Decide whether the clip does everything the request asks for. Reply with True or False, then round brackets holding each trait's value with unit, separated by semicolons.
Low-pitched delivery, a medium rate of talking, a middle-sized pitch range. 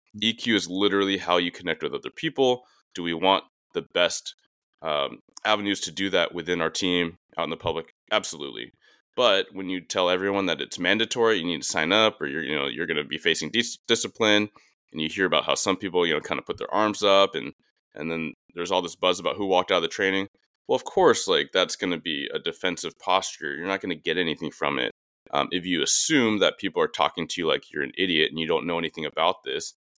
False (100 Hz; 240 wpm; 4.3 semitones)